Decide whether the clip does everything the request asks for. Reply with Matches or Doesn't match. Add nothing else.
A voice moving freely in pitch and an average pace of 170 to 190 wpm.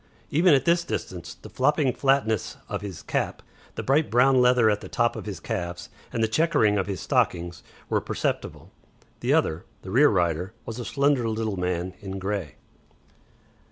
Matches